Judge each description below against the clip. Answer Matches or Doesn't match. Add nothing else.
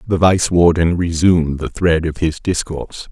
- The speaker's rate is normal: Matches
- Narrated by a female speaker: Doesn't match